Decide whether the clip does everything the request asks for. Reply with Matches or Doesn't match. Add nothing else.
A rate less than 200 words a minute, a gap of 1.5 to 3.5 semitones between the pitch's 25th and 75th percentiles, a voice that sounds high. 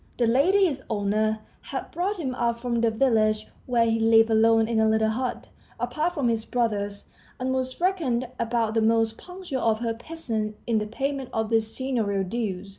Matches